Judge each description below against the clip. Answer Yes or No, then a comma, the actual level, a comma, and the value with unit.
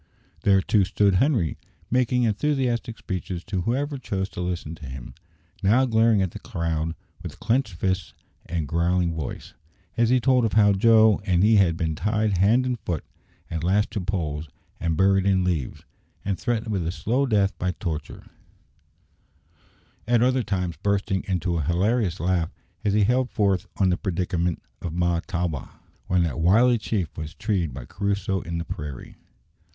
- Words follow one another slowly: No, average, 165 wpm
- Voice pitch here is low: Yes, very low, 95 Hz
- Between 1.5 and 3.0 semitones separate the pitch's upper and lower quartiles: No, average, 4.4 semitones